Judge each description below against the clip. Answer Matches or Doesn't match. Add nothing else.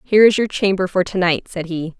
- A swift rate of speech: Matches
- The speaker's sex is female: Matches